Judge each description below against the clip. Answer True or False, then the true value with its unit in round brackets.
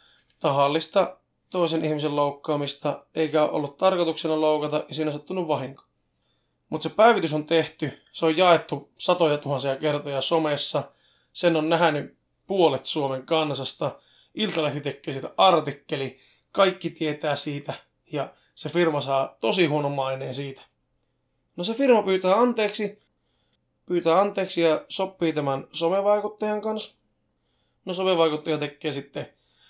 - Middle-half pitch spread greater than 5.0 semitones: False (3.6 semitones)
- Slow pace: False (125 wpm)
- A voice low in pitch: False (155 Hz)